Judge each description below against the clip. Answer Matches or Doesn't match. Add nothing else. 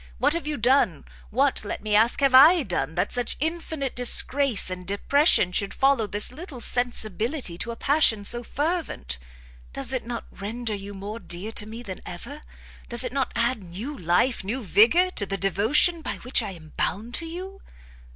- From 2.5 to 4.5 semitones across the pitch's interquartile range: Doesn't match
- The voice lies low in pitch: Doesn't match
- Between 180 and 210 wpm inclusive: Matches